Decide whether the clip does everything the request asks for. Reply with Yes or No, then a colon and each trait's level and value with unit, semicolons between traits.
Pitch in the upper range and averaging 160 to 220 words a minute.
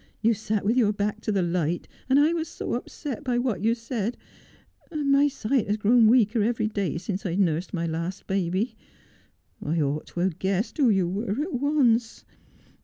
Yes: high, 215 Hz; average, 195 wpm